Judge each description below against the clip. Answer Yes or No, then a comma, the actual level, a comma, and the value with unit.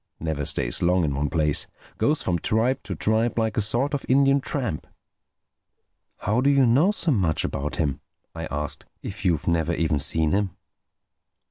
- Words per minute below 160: No, average, 165 wpm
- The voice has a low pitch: Yes, very low, 95 Hz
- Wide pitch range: Yes, wide, 7.7 semitones